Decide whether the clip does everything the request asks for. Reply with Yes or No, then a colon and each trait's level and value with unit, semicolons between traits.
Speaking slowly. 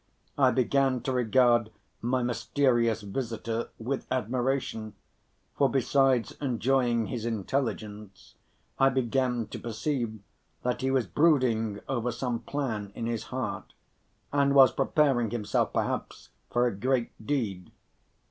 Yes: slow, 120 wpm